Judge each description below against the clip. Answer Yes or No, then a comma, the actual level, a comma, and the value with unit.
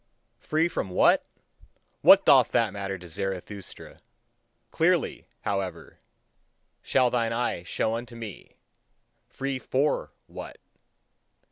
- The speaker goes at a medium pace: No, slow, 105 wpm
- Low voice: Yes, low, 110 Hz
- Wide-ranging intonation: No, average, 4.4 semitones